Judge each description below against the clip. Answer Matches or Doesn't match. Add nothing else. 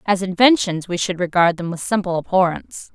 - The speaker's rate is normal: Matches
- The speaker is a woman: Matches